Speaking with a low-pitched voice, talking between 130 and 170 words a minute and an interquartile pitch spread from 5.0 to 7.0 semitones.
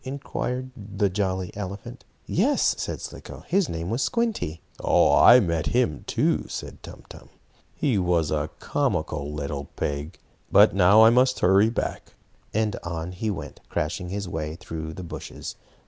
Yes: very low, 95 Hz; average, 150 wpm; wide, 5.6 semitones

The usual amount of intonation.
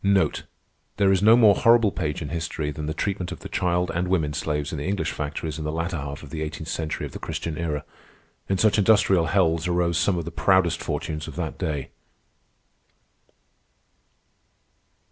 Yes: average, 3.4 semitones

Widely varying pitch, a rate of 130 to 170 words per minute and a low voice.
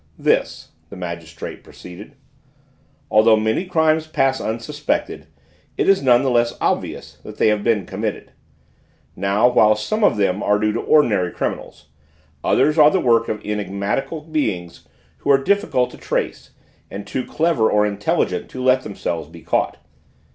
Yes: wide, 5.7 semitones; average, 155 wpm; low, 110 Hz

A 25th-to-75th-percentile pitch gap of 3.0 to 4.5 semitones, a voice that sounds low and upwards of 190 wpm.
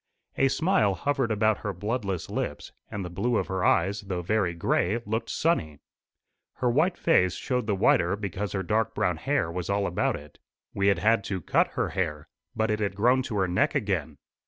Yes: average, 3.7 semitones; low, 100 Hz; average, 200 wpm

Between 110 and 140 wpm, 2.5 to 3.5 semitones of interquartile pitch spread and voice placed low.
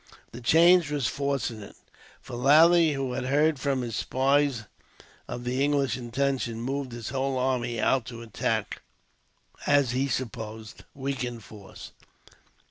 Yes: slow, 135 wpm; average, 2.9 semitones; low, 130 Hz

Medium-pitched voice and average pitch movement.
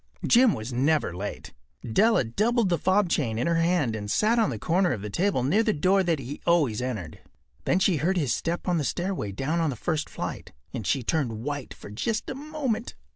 No: medium, 160 Hz; wide, 7.9 semitones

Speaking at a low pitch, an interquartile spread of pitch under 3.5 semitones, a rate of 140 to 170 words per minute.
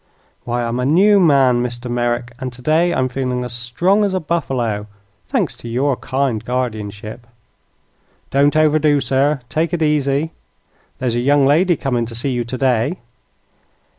No: low, 130 Hz; average, 3.8 semitones; average, 155 wpm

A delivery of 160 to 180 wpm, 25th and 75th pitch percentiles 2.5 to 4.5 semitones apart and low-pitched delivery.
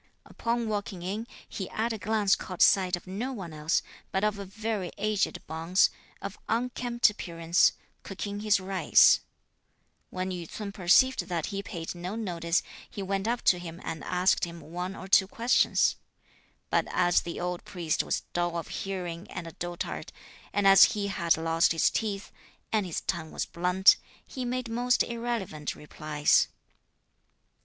No: average, 165 wpm; average, 3.5 semitones; high, 190 Hz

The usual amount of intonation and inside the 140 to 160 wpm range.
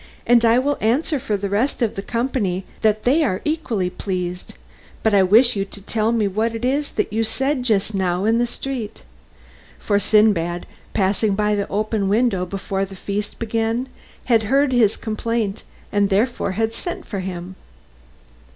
No: average, 3.3 semitones; average, 175 wpm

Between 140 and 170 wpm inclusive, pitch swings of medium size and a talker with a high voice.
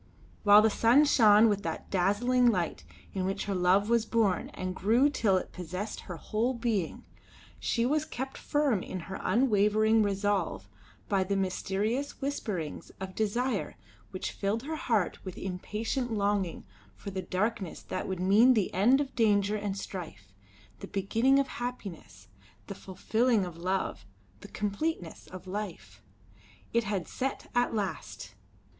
Yes: average, 150 wpm; average, 3.9 semitones; high, 205 Hz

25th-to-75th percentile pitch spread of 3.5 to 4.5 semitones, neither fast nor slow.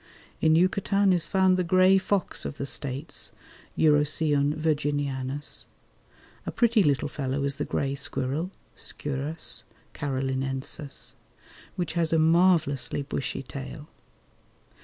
No: average, 3.8 semitones; slow, 115 wpm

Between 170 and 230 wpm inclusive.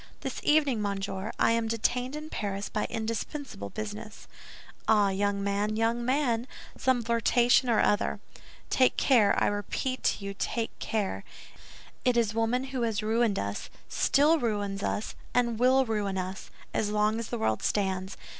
No: average, 155 wpm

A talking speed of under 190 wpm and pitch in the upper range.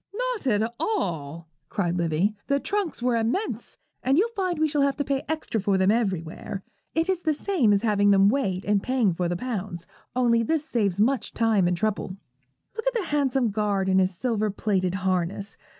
No: average, 195 wpm; high, 215 Hz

